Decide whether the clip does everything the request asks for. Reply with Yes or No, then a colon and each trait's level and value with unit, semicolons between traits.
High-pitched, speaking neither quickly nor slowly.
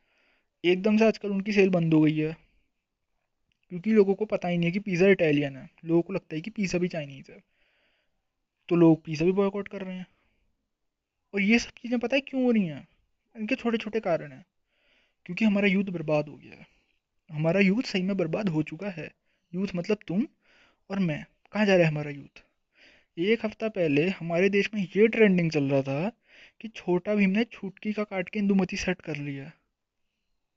No: high, 195 Hz; fast, 200 wpm